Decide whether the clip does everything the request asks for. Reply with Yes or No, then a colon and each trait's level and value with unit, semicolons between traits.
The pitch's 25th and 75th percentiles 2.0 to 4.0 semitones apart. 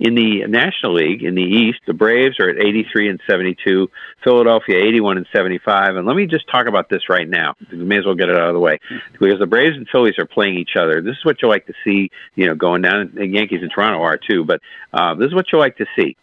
Yes: average, 3.7 semitones